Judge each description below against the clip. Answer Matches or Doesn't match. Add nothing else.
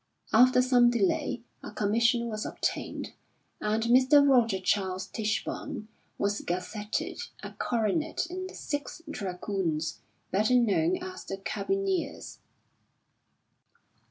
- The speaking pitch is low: Doesn't match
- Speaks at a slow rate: Matches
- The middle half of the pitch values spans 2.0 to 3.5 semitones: Doesn't match